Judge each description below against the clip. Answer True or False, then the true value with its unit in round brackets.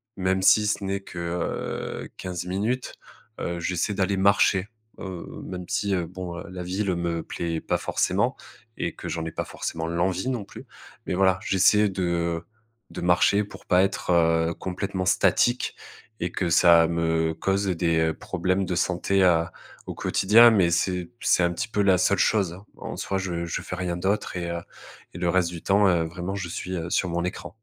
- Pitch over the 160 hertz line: False (90 Hz)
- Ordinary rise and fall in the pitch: False (2.1 semitones)